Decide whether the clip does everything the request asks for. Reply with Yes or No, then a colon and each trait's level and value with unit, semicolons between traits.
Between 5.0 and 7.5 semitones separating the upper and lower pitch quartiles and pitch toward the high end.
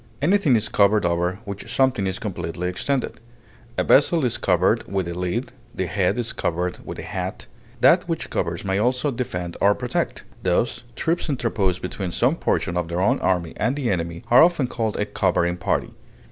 No: wide, 5.6 semitones; low, 100 Hz